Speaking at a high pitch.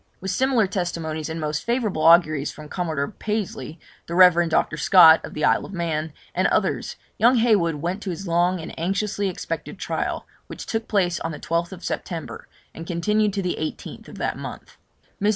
No: medium, 175 Hz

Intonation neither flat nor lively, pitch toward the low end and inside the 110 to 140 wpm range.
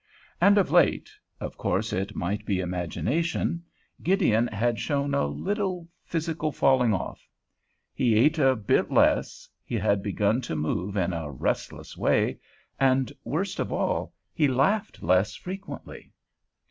No: wide, 8.5 semitones; low, 130 Hz; slow, 135 wpm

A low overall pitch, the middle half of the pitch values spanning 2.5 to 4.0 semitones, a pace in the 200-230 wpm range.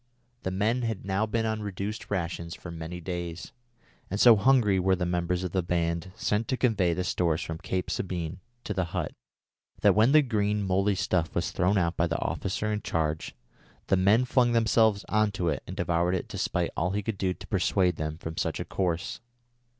Yes: very low, 95 Hz; average, 3.4 semitones; fast, 205 wpm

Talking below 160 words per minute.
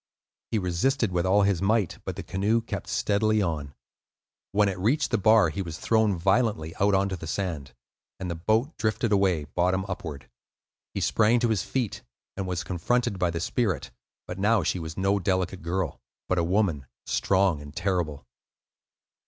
No: average, 175 wpm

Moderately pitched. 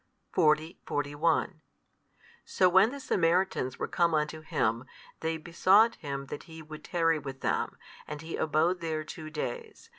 Yes: medium, 160 Hz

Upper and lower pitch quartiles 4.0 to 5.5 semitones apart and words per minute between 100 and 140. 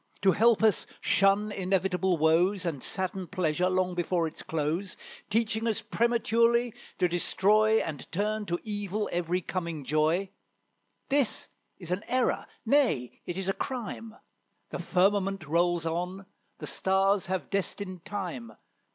No: average, 3.3 semitones; slow, 135 wpm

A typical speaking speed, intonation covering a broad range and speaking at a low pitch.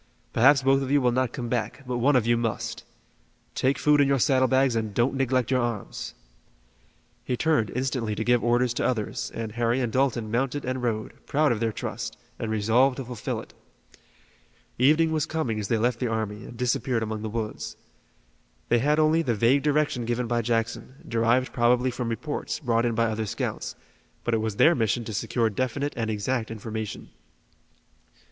No: average, 190 wpm; average, 2.7 semitones; low, 120 Hz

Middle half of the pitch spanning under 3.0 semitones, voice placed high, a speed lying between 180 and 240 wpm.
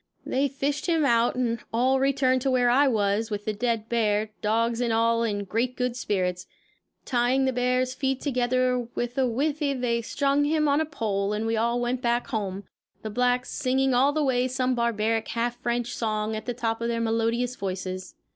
Yes: narrow, 2.4 semitones; high, 240 Hz; average, 195 wpm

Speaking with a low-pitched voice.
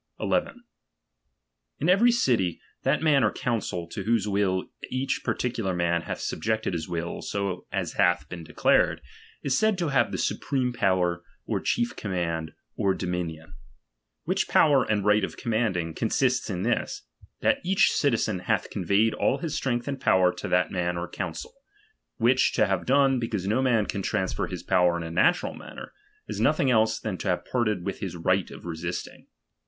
Yes: low, 100 Hz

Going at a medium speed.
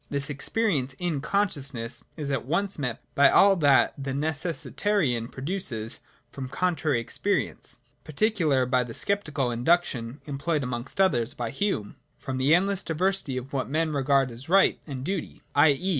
Yes: average, 155 wpm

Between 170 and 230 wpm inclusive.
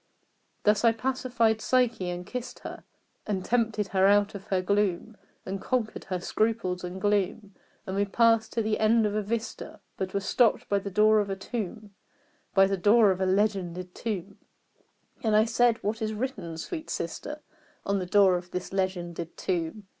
Yes: average, 180 wpm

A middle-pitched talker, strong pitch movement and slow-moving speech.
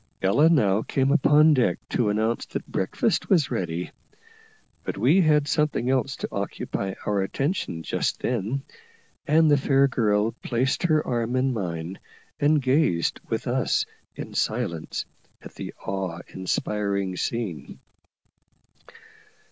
No: low, 120 Hz; wide, 6.7 semitones; slow, 130 wpm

